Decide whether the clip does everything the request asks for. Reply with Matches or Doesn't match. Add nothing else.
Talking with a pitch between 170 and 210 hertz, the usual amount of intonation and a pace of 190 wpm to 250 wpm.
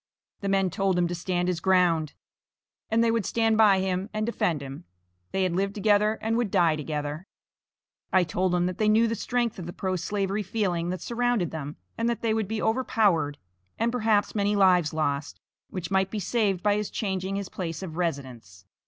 Matches